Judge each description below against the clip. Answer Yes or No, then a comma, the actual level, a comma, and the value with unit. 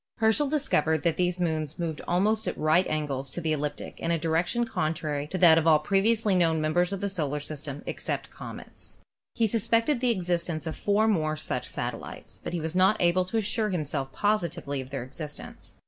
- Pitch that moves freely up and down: No, average, 4.6 semitones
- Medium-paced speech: No, fast, 210 wpm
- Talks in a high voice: No, medium, 170 Hz